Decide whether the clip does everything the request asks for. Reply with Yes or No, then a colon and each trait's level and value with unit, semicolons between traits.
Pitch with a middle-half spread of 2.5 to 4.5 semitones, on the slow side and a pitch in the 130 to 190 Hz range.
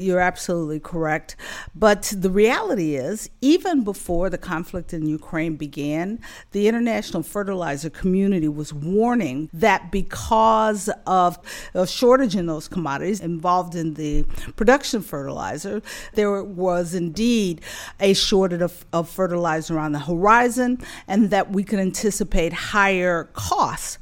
Yes: average, 4.0 semitones; slow, 125 wpm; medium, 185 Hz